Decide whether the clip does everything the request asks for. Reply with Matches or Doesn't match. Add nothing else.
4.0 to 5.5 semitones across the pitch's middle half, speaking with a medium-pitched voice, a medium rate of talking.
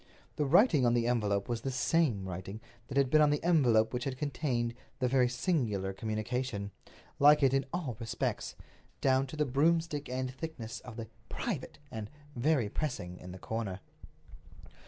Doesn't match